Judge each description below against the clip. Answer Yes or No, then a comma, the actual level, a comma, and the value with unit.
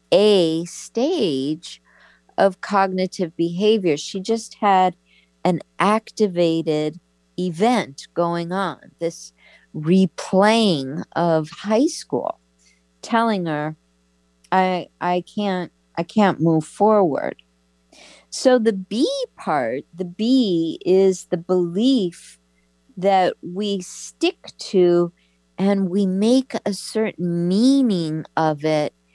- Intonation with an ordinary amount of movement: Yes, average, 4.7 semitones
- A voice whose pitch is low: No, medium, 180 Hz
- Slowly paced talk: Yes, slow, 100 wpm